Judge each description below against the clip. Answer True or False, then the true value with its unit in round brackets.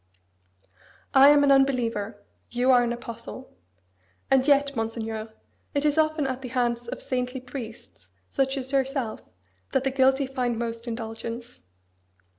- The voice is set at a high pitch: True (250 Hz)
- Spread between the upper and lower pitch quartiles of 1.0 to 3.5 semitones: True (2.6 semitones)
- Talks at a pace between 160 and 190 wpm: False (140 wpm)